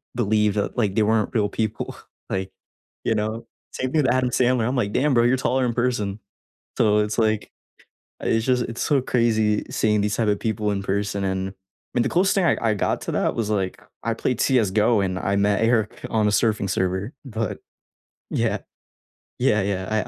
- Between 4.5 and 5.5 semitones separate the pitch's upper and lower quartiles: No, average, 2.9 semitones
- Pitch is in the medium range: No, low, 110 Hz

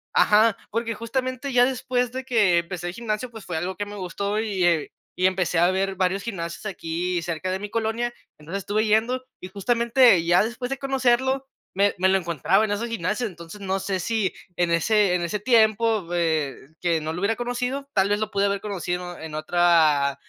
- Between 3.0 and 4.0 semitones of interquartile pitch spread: No, average, 4.6 semitones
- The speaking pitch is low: No, high, 200 Hz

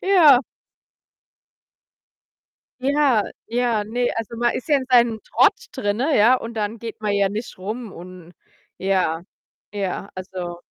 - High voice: Yes, high, 220 Hz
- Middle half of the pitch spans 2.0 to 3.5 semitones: No, average, 4.1 semitones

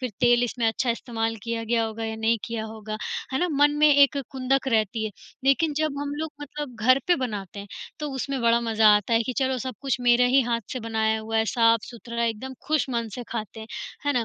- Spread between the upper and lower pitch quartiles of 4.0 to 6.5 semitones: No, average, 2.9 semitones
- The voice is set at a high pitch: Yes, high, 235 Hz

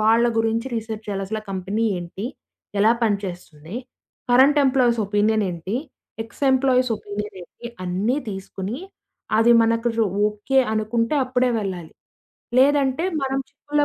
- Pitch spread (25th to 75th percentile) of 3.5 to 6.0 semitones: Yes, average, 4.0 semitones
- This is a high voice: Yes, high, 225 Hz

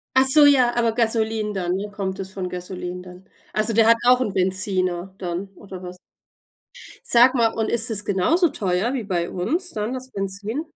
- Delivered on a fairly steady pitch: No, average, 4.2 semitones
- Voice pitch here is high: Yes, high, 210 Hz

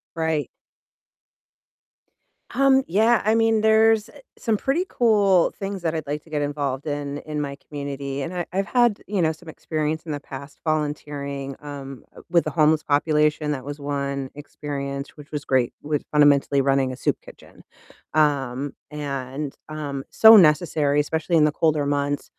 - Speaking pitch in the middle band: Yes, medium, 150 Hz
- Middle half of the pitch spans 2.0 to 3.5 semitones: Yes, average, 2.8 semitones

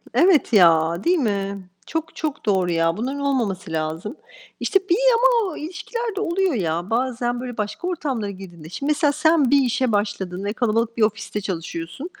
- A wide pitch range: Yes, wide, 8.1 semitones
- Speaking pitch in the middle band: No, high, 230 Hz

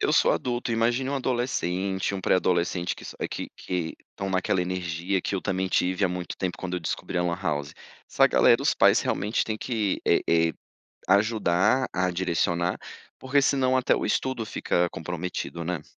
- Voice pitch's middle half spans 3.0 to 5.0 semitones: Yes, average, 4.2 semitones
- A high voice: No, very low, 95 Hz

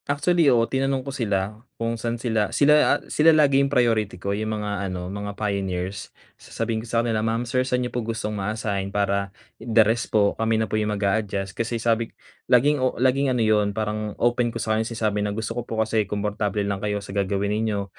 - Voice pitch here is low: Yes, low, 110 Hz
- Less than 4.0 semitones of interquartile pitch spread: Yes, narrow, 2.6 semitones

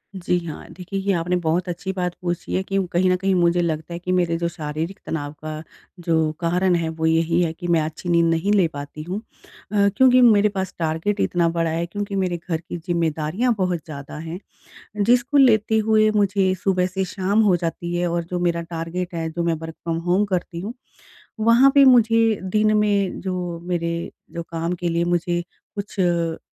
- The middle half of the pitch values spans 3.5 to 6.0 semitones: No, average, 2.9 semitones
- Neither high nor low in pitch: Yes, medium, 175 Hz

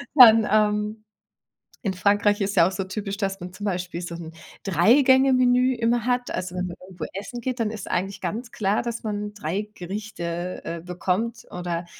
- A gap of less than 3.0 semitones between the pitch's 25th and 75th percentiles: No, average, 4.0 semitones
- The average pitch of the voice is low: No, high, 205 Hz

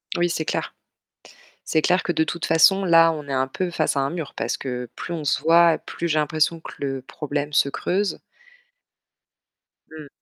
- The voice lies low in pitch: No, medium, 160 Hz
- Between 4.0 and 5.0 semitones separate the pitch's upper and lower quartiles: No, average, 2.9 semitones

